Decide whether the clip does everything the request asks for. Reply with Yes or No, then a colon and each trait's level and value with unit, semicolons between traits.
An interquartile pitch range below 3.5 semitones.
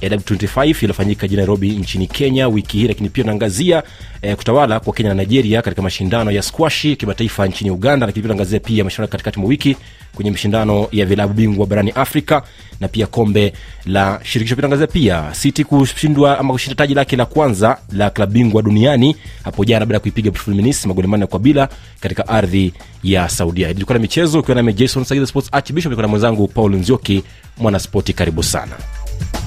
No: average, 4.6 semitones